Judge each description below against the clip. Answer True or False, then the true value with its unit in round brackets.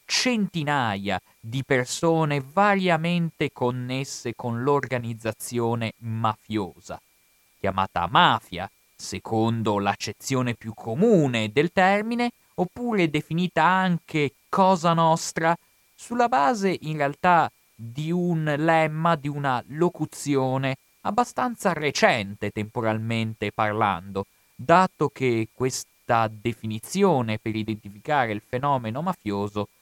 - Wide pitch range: True (7.1 semitones)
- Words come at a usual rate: False (90 wpm)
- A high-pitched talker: False (135 Hz)